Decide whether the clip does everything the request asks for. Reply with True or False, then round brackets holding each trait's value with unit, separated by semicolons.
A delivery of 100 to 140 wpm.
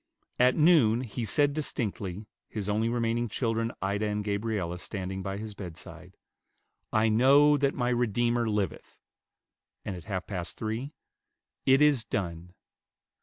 True (135 wpm)